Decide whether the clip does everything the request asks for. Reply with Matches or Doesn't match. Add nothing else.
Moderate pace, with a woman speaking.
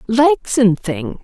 Matches